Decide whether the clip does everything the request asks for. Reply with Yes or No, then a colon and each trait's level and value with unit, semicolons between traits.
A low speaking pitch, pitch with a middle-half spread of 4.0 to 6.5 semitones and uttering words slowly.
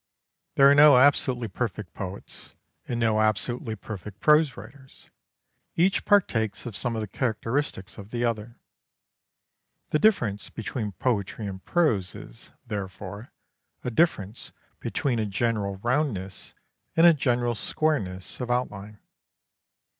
Yes: low, 115 Hz; average, 4.3 semitones; slow, 125 wpm